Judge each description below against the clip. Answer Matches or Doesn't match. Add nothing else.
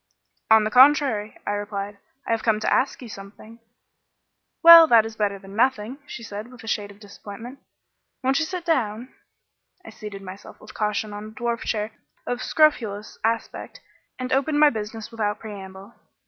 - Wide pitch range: Doesn't match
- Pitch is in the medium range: Doesn't match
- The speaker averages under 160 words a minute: Doesn't match